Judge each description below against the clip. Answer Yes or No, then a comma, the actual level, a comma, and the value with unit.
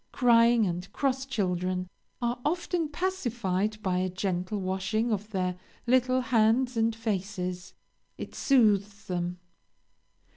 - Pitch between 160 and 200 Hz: No, high, 215 Hz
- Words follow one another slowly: Yes, slow, 115 wpm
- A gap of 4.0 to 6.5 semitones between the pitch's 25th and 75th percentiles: Yes, average, 4.8 semitones